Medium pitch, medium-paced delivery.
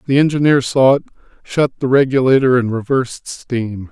No: low, 130 Hz; average, 155 wpm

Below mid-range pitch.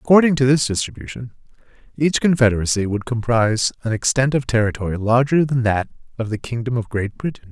Yes: low, 120 Hz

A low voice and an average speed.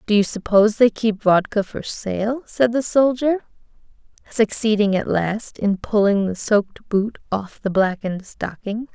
No: high, 210 Hz; average, 155 wpm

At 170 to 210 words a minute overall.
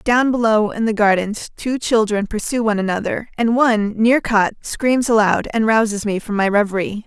Yes: average, 185 wpm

